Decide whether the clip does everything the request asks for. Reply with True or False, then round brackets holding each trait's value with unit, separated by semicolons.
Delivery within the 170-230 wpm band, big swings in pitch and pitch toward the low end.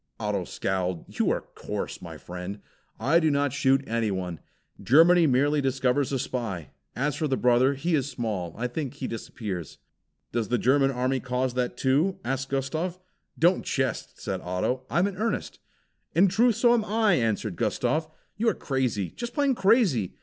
True (180 wpm; 5.8 semitones; 130 Hz)